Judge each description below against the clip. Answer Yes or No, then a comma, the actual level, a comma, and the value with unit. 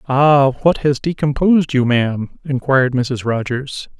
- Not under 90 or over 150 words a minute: Yes, slow, 135 wpm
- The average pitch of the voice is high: No, low, 135 Hz